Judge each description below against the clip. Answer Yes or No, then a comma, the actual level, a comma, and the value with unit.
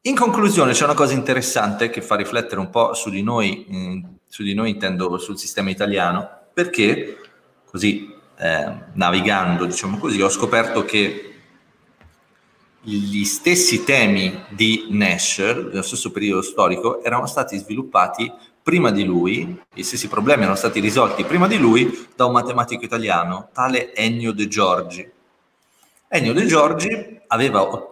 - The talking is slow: No, average, 145 wpm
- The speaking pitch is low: Yes, low, 115 Hz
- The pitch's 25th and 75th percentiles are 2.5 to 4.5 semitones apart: No, average, 5.1 semitones